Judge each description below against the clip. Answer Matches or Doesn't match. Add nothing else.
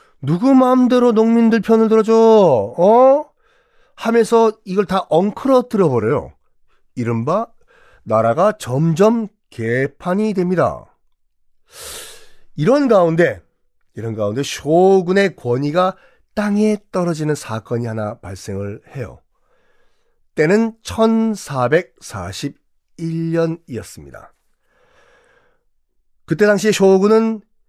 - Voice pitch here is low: Doesn't match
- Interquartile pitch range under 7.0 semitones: Doesn't match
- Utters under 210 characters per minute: Matches